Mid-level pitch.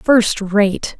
No: high, 210 Hz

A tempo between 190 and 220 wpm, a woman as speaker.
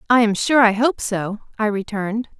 Yes: average, 200 wpm; female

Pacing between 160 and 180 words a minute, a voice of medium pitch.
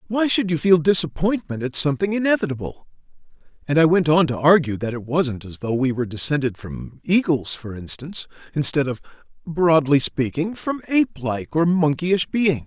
Yes: average, 170 wpm; medium, 155 Hz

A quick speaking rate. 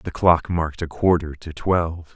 No: average, 195 wpm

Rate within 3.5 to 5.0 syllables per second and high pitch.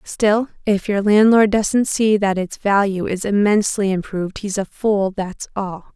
Yes: 4.4 syllables/s; high, 200 Hz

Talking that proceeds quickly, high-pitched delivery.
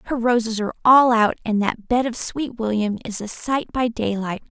Yes: fast, 210 wpm; high, 230 Hz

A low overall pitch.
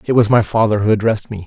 Yes: low, 110 Hz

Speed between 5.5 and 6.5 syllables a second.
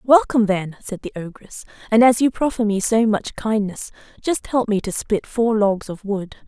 No: 4.8 syllables/s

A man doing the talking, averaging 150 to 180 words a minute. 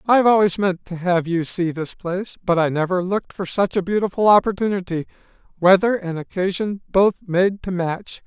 Yes: male; average, 175 wpm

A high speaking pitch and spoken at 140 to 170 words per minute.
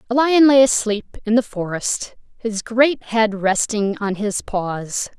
Yes: high, 220 Hz; average, 160 wpm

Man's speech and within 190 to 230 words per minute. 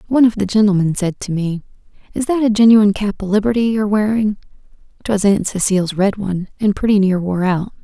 No: female; average, 200 wpm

